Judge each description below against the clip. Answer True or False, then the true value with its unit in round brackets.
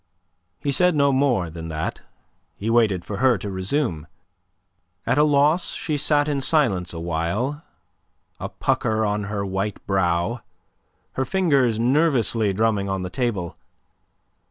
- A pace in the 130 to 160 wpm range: True (135 wpm)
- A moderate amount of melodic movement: False (6.7 semitones)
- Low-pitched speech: True (110 Hz)